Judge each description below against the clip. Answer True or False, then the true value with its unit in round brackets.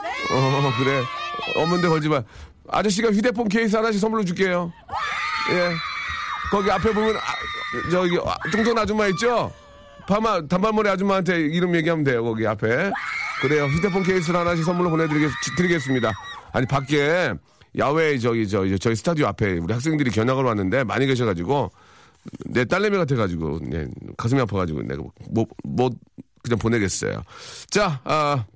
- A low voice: False (150 Hz)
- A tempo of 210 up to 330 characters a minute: False (350 characters per minute)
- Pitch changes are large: True (8.2 semitones)